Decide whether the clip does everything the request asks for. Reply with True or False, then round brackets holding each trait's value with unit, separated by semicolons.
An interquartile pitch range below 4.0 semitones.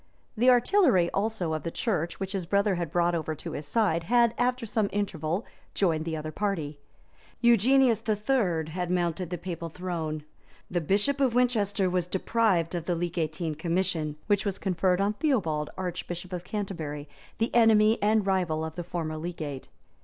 False (4.4 semitones)